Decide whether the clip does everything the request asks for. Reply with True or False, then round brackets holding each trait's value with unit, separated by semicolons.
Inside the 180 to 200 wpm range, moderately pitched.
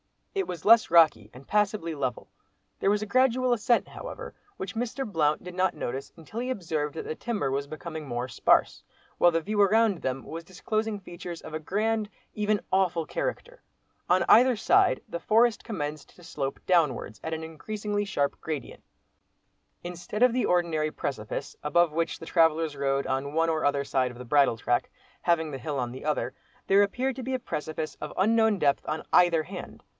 True (190 wpm; 170 Hz)